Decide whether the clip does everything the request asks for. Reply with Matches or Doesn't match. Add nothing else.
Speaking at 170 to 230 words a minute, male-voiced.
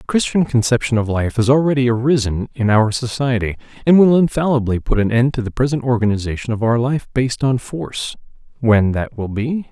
Matches